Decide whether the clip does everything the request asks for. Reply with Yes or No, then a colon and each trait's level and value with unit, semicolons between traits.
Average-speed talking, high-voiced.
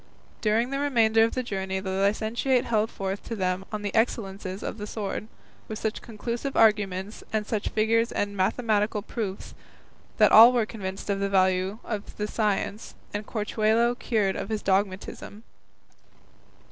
Yes: average, 160 wpm; high, 210 Hz